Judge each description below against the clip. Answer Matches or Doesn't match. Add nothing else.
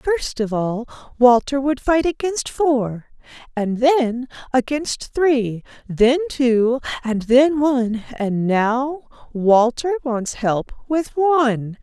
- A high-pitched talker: Matches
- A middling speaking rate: Doesn't match